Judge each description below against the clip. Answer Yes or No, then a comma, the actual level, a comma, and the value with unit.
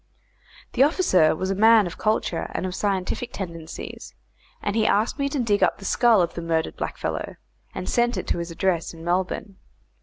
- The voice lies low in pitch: No, high, 195 Hz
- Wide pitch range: No, average, 4.6 semitones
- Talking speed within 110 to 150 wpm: No, average, 190 wpm